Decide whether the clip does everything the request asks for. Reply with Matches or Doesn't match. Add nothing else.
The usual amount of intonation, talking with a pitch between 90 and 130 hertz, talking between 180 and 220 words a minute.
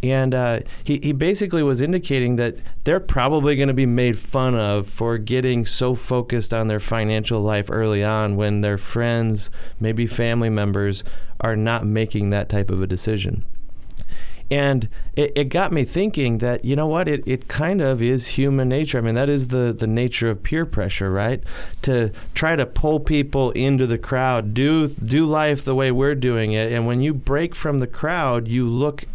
Matches